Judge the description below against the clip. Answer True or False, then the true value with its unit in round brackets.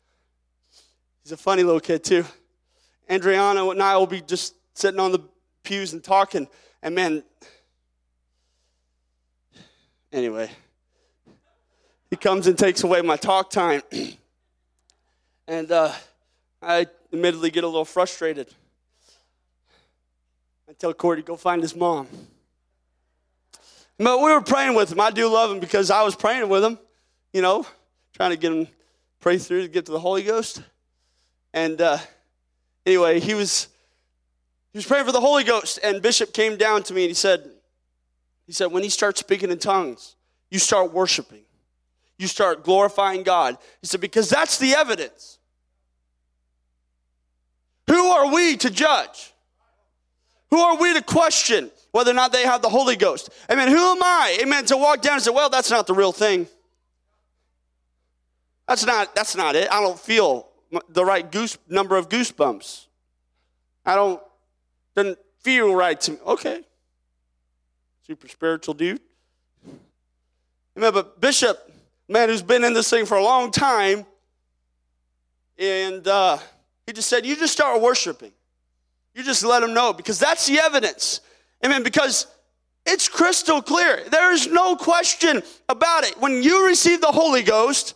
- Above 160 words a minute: False (155 wpm)